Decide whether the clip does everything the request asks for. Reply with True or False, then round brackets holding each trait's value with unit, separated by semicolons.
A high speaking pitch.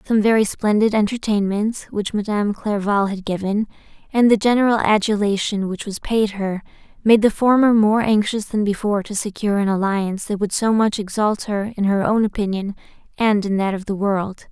True (205 Hz)